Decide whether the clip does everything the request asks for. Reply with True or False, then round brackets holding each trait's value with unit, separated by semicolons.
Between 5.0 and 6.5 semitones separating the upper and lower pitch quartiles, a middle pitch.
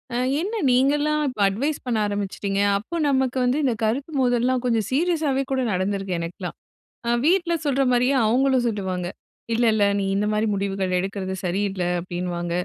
False (5.6 semitones; 225 Hz)